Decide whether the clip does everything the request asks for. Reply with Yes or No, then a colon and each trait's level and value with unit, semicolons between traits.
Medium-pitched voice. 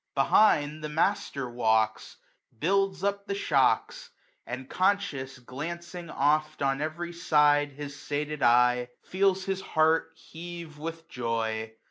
Yes: medium, 150 Hz